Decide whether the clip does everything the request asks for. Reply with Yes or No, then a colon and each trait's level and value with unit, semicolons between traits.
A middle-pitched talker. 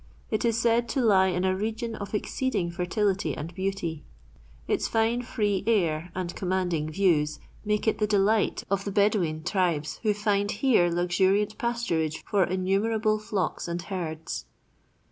No: high, 195 Hz